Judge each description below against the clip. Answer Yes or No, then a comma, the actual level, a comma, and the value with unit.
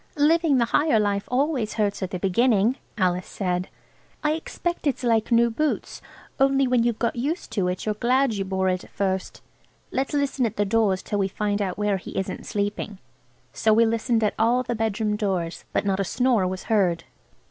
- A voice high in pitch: Yes, high, 215 Hz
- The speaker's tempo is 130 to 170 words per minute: No, average, 200 wpm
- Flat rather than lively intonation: No, average, 4.3 semitones